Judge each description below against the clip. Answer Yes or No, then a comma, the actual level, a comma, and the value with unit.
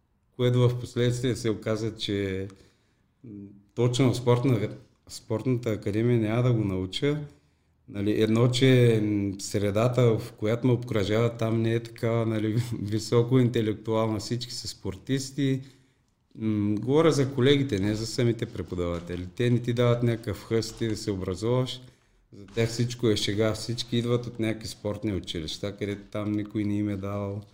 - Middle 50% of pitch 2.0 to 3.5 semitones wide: Yes, average, 2.8 semitones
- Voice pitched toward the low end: Yes, low, 110 Hz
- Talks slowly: No, average, 150 wpm